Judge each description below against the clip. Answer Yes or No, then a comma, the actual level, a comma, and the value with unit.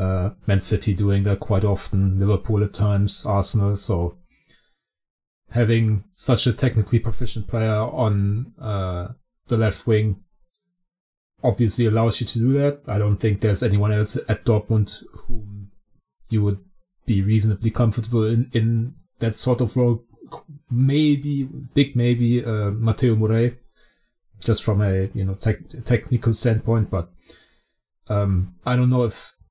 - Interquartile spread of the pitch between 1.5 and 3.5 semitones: Yes, average, 3.1 semitones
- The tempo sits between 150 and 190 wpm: No, average, 140 wpm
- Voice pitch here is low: Yes, low, 110 Hz